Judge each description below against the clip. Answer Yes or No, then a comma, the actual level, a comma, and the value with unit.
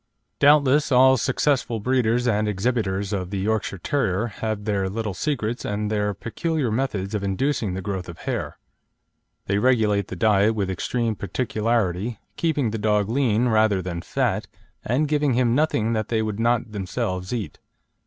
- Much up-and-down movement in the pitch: No, average, 3.6 semitones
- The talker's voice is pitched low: Yes, low, 110 Hz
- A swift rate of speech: No, average, 160 wpm